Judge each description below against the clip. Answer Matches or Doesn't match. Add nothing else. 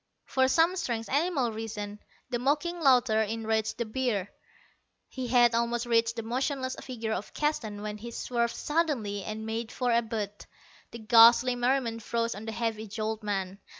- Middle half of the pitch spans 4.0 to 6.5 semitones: Doesn't match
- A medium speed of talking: Matches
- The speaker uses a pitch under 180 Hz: Doesn't match